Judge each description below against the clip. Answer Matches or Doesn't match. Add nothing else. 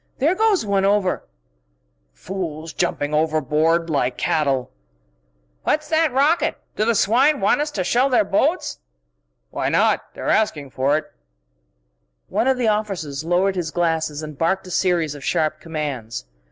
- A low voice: Doesn't match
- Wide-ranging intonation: Matches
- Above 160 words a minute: Doesn't match